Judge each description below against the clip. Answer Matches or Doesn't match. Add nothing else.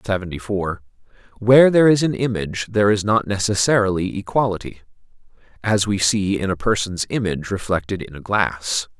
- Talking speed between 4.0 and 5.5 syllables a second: Doesn't match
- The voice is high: Doesn't match